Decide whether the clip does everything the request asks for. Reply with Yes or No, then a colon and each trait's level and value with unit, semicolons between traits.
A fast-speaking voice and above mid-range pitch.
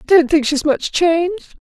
Yes: fast, 220 wpm; very high, 325 Hz